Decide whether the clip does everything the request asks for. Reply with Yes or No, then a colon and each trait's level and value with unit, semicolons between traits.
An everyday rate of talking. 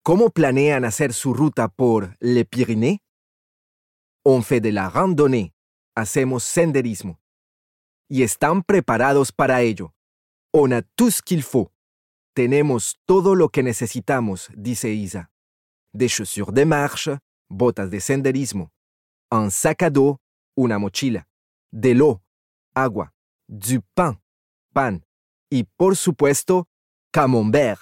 No: slow, 115 wpm